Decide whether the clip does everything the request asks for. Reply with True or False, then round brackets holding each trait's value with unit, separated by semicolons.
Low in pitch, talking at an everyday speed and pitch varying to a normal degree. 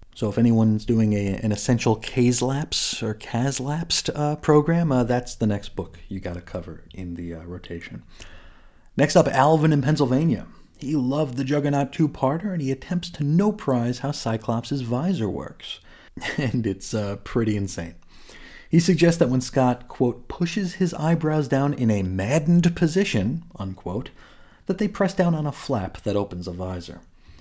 False (125 Hz; 175 wpm; 7.5 semitones)